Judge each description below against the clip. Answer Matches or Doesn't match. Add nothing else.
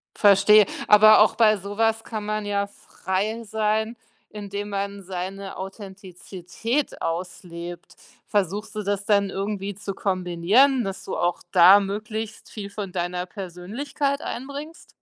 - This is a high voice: Matches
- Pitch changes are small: Matches